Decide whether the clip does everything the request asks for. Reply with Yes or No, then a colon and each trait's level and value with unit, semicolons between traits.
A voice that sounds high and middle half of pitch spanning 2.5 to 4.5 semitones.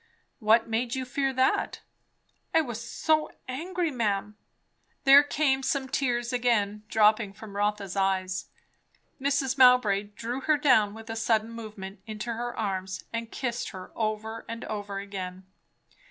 Yes: high, 225 Hz; average, 3.9 semitones